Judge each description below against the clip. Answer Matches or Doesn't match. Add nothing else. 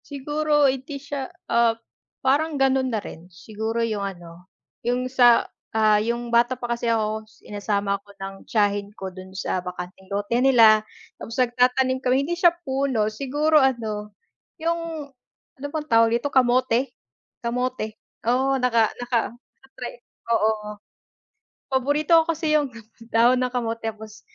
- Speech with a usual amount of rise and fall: Matches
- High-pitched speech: Matches